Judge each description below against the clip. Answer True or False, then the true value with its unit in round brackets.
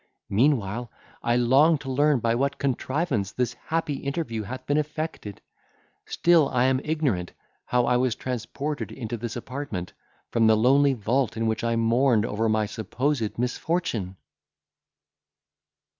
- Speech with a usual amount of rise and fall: True (3.9 semitones)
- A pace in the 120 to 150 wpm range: True (140 wpm)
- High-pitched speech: False (125 Hz)